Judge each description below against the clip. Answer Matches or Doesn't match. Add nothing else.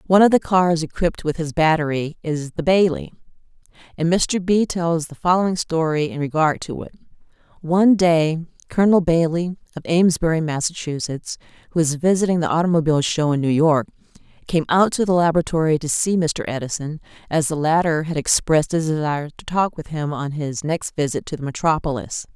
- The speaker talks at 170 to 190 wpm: Matches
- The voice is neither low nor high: Matches